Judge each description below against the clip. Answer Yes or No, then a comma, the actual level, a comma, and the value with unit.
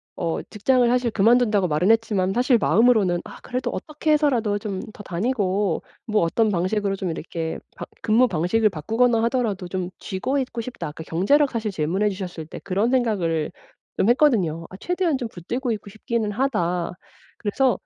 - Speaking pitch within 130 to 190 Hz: No, high, 210 Hz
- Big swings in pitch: No, average, 5.0 semitones